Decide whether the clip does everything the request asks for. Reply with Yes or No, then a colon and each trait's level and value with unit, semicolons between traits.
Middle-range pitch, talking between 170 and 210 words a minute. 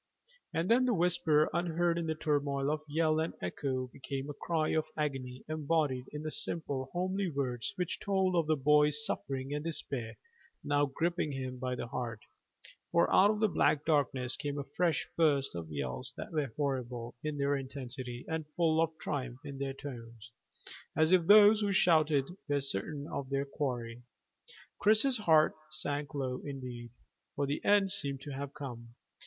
Yes: medium, 145 Hz; average, 175 wpm